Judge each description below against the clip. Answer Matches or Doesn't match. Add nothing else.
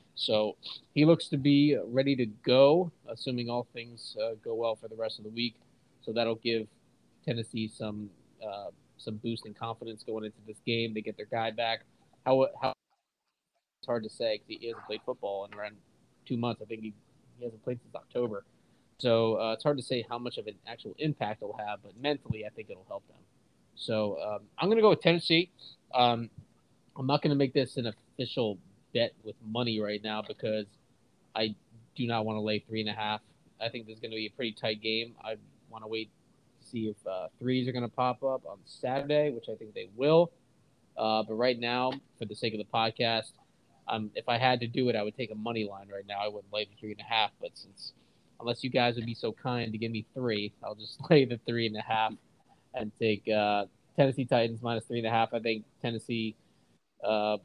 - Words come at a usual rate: Doesn't match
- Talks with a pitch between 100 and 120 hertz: Matches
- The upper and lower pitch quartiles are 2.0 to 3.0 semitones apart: Matches